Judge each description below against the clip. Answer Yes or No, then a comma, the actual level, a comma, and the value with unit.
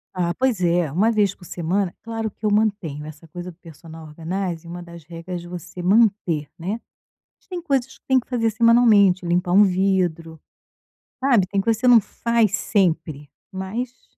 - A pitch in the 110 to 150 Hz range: No, medium, 185 Hz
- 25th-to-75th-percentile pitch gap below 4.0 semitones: No, average, 4.6 semitones